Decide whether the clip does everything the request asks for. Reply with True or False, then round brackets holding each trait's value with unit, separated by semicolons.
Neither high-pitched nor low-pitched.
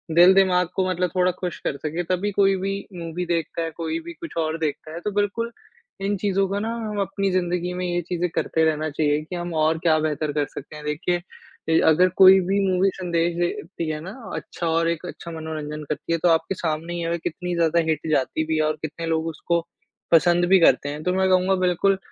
True (175 Hz)